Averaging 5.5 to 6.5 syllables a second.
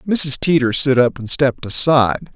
No: 5.2 syllables/s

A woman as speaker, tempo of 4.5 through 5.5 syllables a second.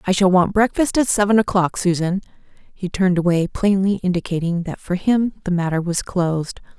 Yes: female; 5.3 syllables/s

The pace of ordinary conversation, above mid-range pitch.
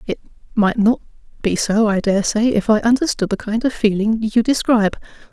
Yes: average, 190 wpm; high, 220 Hz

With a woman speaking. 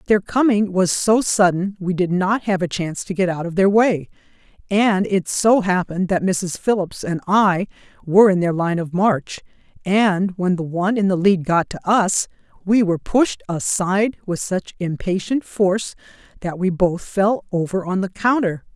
Yes: female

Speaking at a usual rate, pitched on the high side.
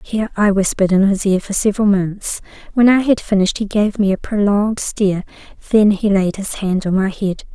No: fast, 215 wpm; high, 200 Hz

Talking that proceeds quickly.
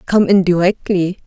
No: average, 140 wpm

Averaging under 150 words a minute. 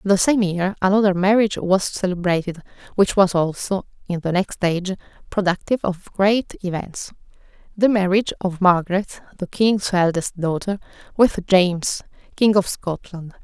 Yes: average, 140 wpm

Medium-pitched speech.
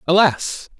Yes: medium, 175 Hz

